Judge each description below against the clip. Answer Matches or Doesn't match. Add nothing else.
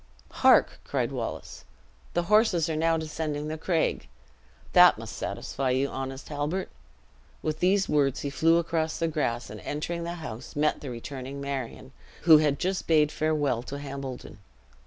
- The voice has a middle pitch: Matches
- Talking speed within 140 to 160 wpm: Matches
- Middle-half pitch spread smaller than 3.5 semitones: Matches